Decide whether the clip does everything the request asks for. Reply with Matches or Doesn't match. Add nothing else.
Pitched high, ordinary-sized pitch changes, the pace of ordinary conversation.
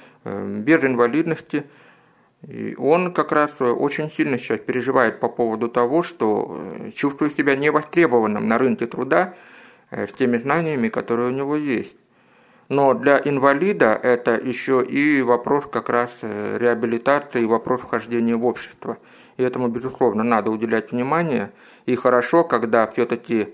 Doesn't match